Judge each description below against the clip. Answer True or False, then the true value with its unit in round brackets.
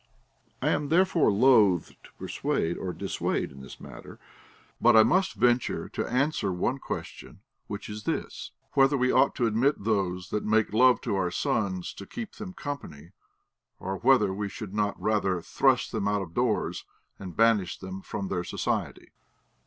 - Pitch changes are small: False (5.0 semitones)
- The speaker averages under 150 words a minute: False (170 wpm)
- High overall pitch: False (105 Hz)